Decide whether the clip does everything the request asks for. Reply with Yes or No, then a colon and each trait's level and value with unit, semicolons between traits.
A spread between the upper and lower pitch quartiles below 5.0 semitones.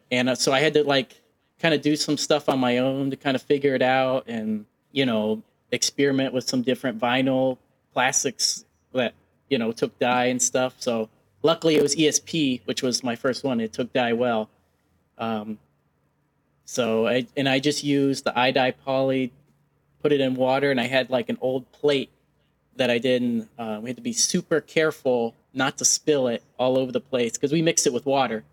Yes: narrow, 2.4 semitones